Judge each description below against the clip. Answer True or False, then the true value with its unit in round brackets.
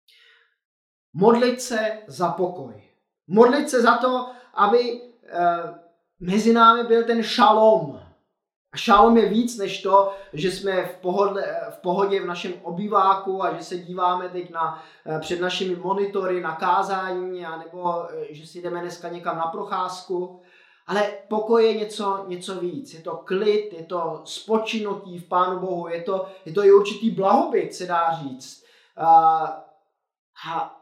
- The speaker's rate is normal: True (145 wpm)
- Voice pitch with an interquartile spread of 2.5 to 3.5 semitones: True (3.2 semitones)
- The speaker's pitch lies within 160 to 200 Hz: True (185 Hz)